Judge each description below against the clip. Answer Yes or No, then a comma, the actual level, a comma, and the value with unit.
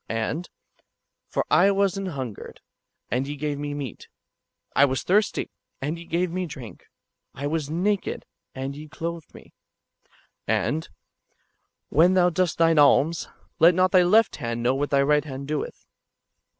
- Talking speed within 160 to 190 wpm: Yes, average, 170 wpm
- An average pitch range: Yes, average, 4.3 semitones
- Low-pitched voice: No, medium, 155 Hz